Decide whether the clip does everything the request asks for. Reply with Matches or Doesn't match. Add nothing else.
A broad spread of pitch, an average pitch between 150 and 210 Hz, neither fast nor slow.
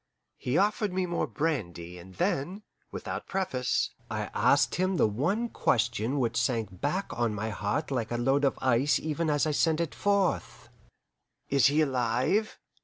Doesn't match